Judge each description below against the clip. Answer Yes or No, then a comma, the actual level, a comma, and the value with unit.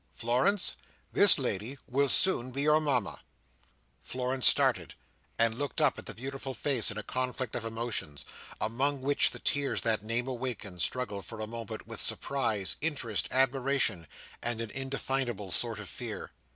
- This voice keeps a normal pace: Yes, average, 155 wpm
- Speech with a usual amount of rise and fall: Yes, average, 3.4 semitones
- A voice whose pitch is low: Yes, low, 125 Hz